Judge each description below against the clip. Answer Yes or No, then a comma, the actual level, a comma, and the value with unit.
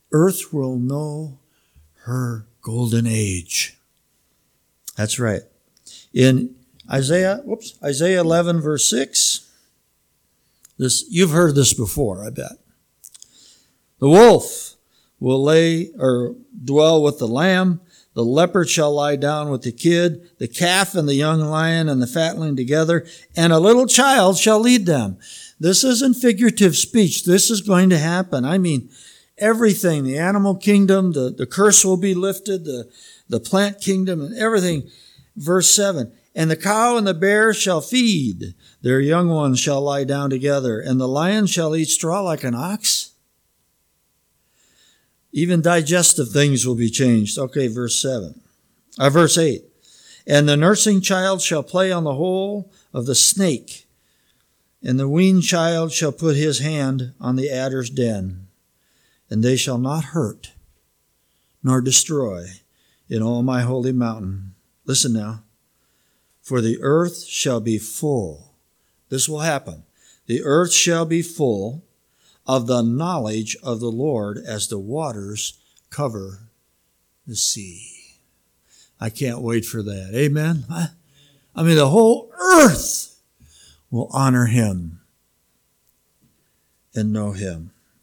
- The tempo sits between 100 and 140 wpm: Yes, slow, 135 wpm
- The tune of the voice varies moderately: No, wide, 6.8 semitones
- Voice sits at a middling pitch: Yes, medium, 145 Hz